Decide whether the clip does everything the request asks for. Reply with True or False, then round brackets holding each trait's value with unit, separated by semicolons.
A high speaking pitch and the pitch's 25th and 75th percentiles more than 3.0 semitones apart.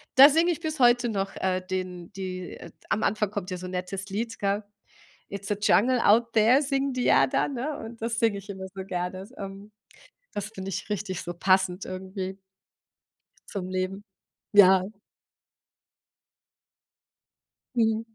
True (200 Hz; 3.5 semitones)